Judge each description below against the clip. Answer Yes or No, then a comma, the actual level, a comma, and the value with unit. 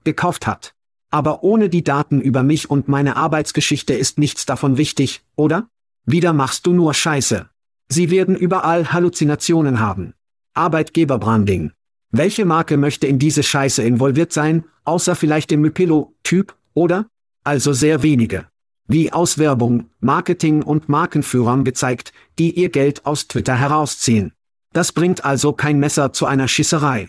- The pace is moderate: Yes, average, 140 wpm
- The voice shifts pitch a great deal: No, average, 3.4 semitones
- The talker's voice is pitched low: No, medium, 150 Hz